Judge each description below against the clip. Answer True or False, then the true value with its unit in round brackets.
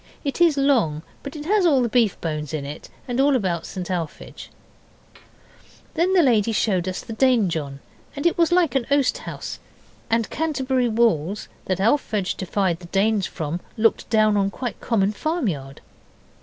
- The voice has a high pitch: True (220 Hz)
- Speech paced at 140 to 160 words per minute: False (170 wpm)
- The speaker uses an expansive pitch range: True (7.1 semitones)